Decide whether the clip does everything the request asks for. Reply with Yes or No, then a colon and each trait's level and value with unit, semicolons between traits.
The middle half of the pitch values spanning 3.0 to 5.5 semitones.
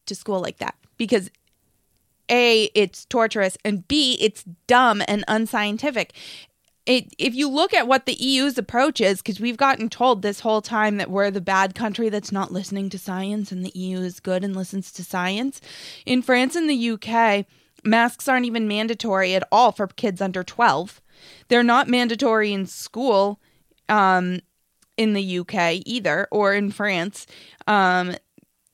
Yes: average, 3.8 semitones